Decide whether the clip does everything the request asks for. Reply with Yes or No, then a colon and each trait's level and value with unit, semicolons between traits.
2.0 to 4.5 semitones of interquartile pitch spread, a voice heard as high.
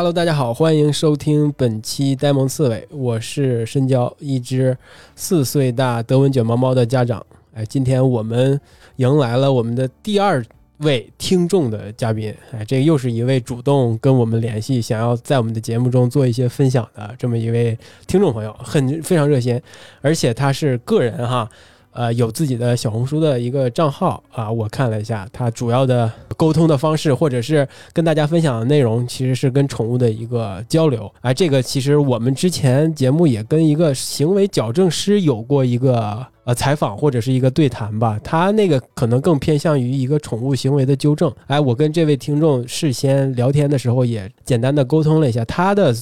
No: average, 3.9 semitones; low, 130 Hz